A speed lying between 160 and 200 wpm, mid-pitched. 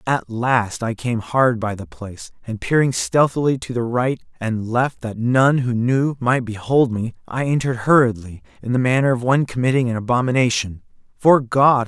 No: average, 180 wpm; low, 120 Hz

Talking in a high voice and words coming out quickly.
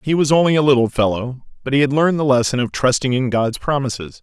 No: low, 130 Hz; fast, 240 wpm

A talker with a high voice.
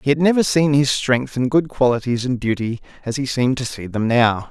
No: low, 130 Hz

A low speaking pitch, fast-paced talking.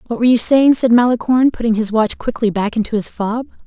No: high, 230 Hz; fast, 230 wpm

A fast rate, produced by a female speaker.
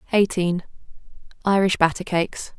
No: slow, 70 wpm; female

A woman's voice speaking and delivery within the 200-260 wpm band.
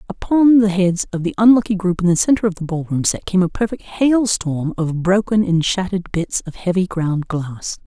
Yes: female; fast, 205 wpm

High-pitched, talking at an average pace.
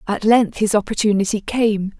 Yes: high, 210 Hz; average, 150 wpm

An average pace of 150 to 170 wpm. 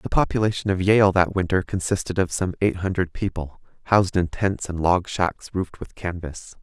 No: average, 190 wpm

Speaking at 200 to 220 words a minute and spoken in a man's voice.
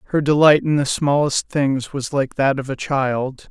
Yes: fast, 205 wpm; male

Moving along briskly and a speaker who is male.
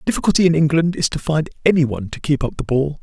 Yes: fast, 280 wpm; male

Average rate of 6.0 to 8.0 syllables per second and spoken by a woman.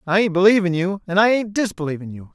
No: 6.5 syllables/s; male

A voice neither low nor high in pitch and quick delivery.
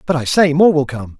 Yes: medium, 150 Hz; fast, 300 wpm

